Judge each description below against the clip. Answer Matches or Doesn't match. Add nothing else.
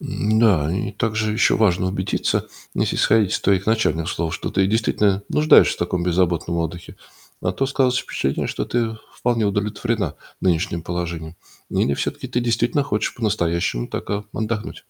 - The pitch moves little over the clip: Doesn't match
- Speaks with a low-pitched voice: Matches